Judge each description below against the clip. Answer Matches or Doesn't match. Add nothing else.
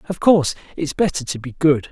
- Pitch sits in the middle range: Matches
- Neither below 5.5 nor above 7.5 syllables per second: Matches